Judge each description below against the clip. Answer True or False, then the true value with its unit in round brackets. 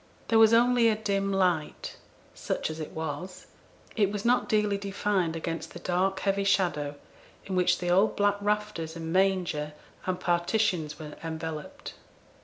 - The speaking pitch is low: False (185 Hz)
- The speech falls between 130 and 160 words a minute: True (155 wpm)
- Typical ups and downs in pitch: True (3.9 semitones)